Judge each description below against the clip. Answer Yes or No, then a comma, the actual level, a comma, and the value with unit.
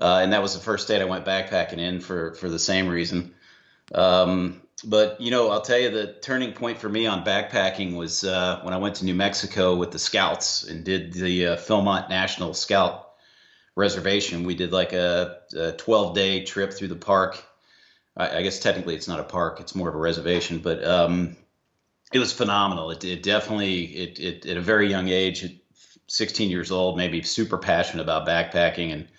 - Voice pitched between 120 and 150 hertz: No, very low, 90 Hz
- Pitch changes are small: Yes, narrow, 2.1 semitones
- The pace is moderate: Yes, average, 195 wpm